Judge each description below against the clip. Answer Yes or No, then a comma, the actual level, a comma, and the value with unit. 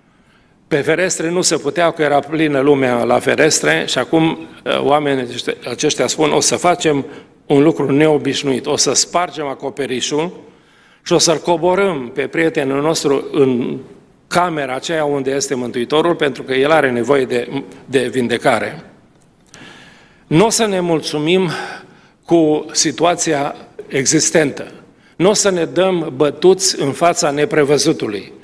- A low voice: No, medium, 150 Hz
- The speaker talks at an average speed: Yes, average, 135 wpm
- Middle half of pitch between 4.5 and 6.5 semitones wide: No, average, 3.4 semitones